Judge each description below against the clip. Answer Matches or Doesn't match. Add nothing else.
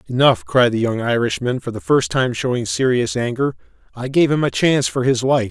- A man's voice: Matches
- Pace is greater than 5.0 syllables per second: Matches